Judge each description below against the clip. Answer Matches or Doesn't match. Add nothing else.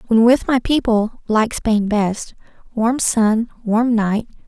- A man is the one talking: Doesn't match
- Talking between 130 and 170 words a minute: Matches